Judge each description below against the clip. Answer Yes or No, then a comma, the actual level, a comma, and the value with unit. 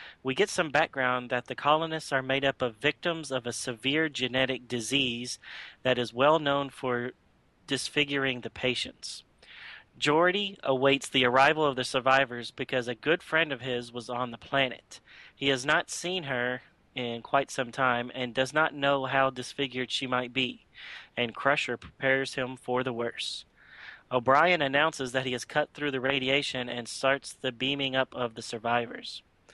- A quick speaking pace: No, average, 170 wpm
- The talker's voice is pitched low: Yes, low, 130 Hz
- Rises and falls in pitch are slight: Yes, narrow, 2.0 semitones